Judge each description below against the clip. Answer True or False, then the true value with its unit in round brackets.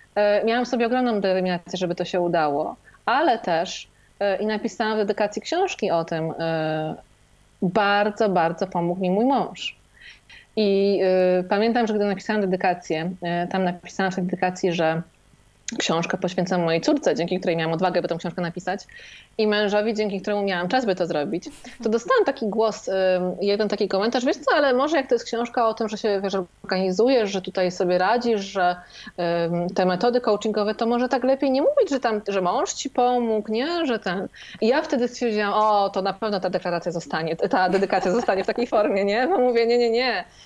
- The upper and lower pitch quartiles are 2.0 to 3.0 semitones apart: False (4.2 semitones)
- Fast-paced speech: True (185 wpm)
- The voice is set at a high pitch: True (200 Hz)